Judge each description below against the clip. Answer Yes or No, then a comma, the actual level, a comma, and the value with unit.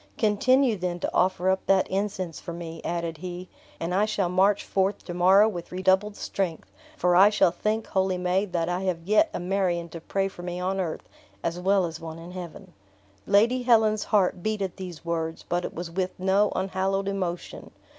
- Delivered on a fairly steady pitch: Yes, narrow, 2.2 semitones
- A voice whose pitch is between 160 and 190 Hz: Yes, medium, 185 Hz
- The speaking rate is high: No, average, 195 wpm